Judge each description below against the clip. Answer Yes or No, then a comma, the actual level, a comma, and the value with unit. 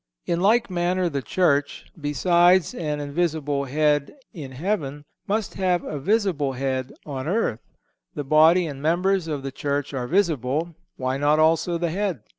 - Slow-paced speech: No, average, 155 wpm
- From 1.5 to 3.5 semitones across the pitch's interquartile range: No, average, 3.9 semitones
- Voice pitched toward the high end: No, medium, 155 Hz